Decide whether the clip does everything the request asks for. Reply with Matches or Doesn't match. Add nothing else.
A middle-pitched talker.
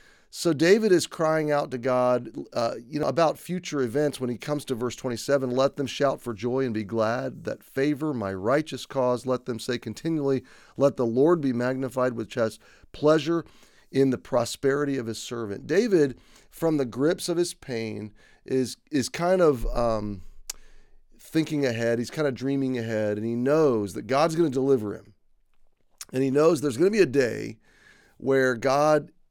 Doesn't match